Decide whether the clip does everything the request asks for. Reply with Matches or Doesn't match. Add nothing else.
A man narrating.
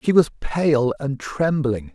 Matches